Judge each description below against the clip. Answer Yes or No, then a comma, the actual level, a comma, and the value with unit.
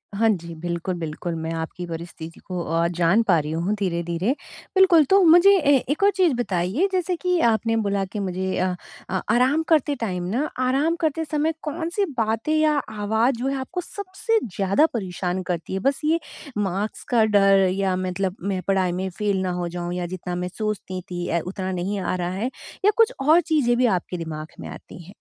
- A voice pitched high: Yes, high, 200 Hz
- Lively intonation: Yes, wide, 8.2 semitones